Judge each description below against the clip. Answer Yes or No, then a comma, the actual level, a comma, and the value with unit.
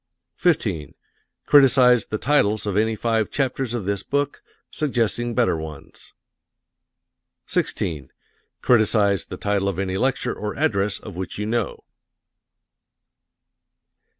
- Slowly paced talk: Yes, slow, 115 wpm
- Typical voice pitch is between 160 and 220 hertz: No, low, 110 Hz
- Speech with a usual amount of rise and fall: Yes, average, 4.0 semitones